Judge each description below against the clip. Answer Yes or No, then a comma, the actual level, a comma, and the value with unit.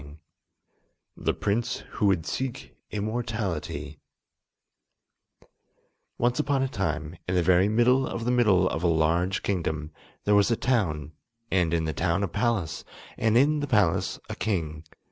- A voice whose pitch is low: Yes, very low, 95 Hz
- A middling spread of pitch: No, wide, 6.1 semitones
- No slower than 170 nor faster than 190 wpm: No, average, 150 wpm